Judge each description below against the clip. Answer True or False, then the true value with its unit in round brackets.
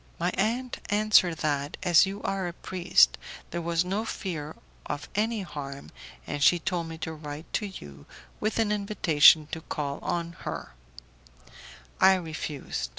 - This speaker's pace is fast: False (155 wpm)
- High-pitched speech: False (170 Hz)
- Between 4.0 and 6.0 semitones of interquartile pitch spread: True (4.5 semitones)